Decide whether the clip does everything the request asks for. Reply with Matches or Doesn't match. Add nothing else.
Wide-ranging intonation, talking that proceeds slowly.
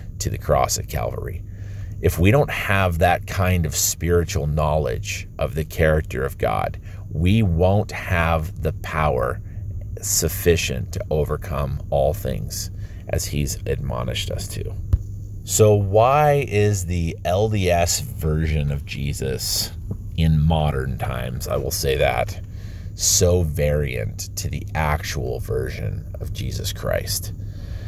Doesn't match